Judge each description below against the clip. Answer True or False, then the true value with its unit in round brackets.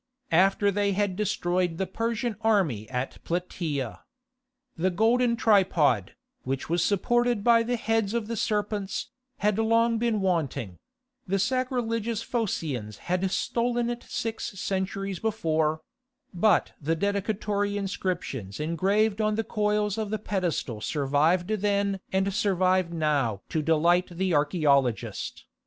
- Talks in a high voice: True (195 Hz)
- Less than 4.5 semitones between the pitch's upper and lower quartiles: False (4.9 semitones)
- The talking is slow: True (125 wpm)